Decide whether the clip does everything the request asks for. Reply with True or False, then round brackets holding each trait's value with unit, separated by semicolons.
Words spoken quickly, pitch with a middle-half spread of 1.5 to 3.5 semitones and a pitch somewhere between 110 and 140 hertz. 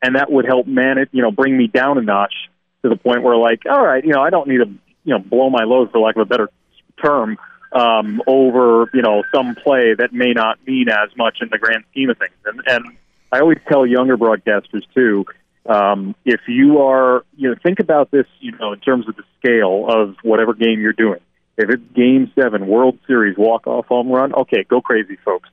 True (230 wpm; 2.9 semitones; 125 Hz)